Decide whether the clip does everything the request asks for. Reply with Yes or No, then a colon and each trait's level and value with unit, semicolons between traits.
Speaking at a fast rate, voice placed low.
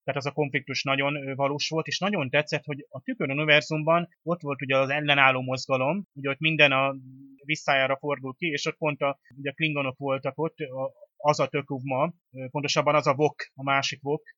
No: fast, 190 wpm; medium, 145 Hz